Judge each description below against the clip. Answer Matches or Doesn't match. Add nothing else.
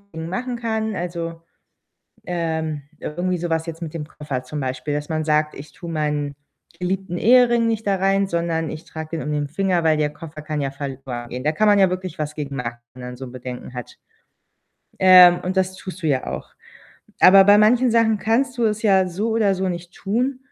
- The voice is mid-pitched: Matches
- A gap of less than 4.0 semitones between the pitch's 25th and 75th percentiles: Doesn't match